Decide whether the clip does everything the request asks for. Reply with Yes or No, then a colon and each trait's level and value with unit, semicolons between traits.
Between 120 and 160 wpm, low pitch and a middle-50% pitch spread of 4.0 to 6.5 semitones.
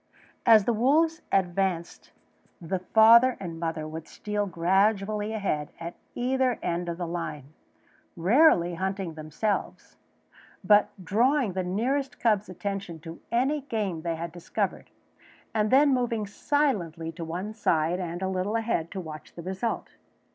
No: average, 140 wpm; high, 190 Hz; average, 4.9 semitones